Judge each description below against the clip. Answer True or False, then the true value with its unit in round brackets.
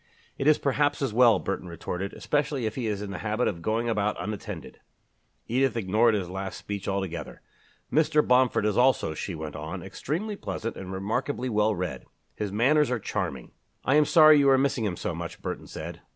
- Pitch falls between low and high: False (110 Hz)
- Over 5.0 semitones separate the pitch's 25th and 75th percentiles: True (5.5 semitones)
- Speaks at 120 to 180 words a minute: False (195 wpm)